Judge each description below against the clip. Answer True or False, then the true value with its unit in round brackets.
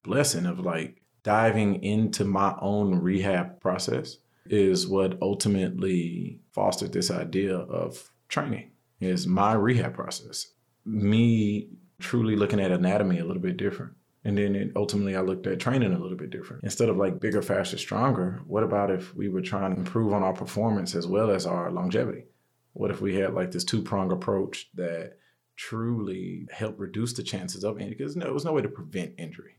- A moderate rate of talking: True (185 wpm)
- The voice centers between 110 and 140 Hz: False (100 Hz)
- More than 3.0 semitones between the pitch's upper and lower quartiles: False (2.7 semitones)